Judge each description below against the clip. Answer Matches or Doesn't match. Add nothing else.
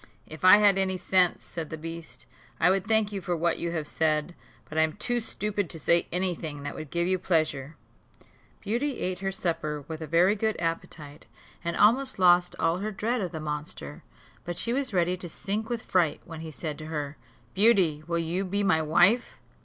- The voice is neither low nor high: Matches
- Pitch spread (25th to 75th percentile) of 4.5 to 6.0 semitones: Doesn't match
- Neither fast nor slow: Doesn't match